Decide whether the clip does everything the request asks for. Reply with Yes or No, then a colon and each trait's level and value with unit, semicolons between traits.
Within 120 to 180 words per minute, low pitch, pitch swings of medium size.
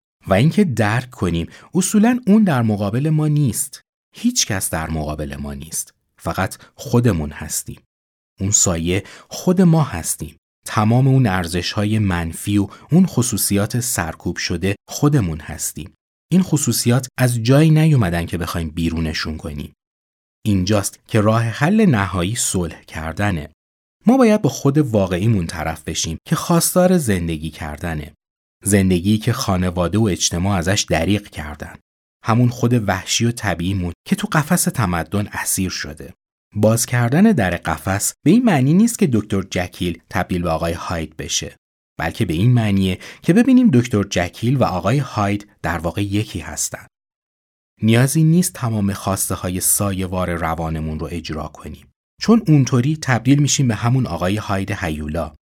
No: average, 145 wpm; low, 100 Hz; wide, 6.7 semitones